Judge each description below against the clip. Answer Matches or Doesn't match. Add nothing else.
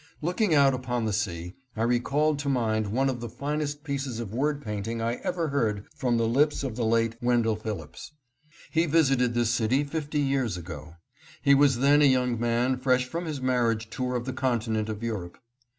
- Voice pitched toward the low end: Matches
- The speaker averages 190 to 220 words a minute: Matches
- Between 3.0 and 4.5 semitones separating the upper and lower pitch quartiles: Matches